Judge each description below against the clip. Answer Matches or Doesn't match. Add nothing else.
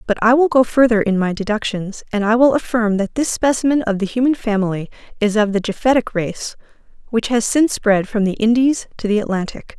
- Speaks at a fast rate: Matches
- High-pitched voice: Matches